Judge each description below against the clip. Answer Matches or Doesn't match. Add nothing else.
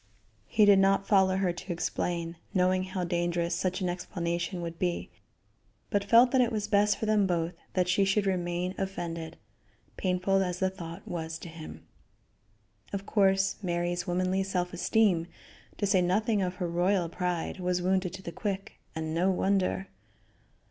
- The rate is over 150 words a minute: Matches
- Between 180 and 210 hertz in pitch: Matches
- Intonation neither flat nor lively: Doesn't match